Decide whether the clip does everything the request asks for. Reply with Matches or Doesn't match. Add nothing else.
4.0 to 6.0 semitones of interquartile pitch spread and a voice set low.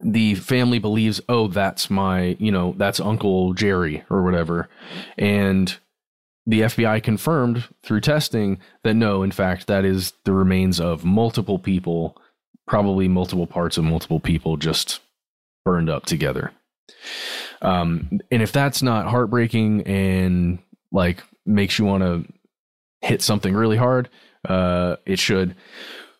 Doesn't match